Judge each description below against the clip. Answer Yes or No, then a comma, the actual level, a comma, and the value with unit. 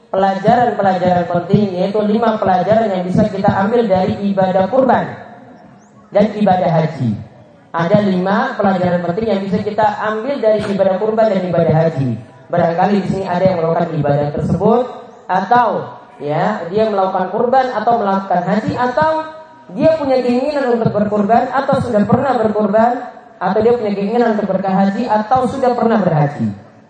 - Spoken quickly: Yes, fast, 145 wpm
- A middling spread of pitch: Yes, average, 4.2 semitones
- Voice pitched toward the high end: Yes, high, 210 Hz